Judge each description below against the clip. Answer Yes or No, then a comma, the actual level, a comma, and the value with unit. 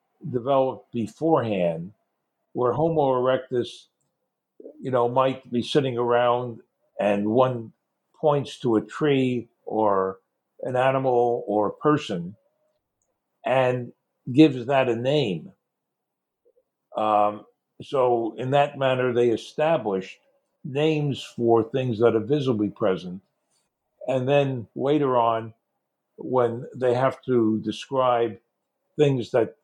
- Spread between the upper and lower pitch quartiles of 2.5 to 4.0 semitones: Yes, average, 3.6 semitones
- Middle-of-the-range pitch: No, low, 125 Hz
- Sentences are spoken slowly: Yes, slow, 105 wpm